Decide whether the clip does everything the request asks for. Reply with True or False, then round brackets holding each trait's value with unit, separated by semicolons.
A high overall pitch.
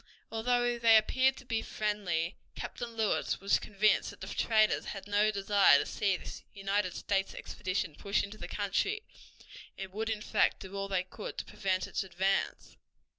True (205 Hz)